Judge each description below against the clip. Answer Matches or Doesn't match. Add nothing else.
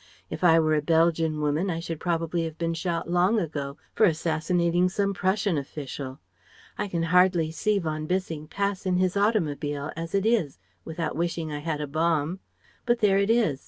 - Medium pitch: Matches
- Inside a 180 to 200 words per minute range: Matches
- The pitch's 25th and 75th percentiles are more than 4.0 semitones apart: Doesn't match